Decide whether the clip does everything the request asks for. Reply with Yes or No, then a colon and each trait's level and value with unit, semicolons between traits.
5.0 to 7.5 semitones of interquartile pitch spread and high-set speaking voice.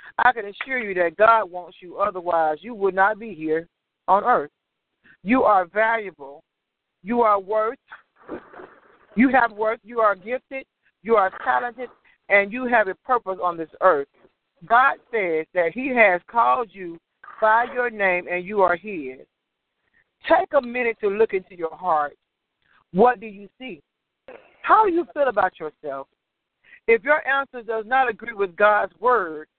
Yes: wide, 5.4 semitones; high, 210 Hz